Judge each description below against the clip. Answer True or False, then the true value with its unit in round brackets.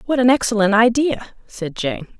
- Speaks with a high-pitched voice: True (230 Hz)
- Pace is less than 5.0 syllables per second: True (4.7 syllables/s)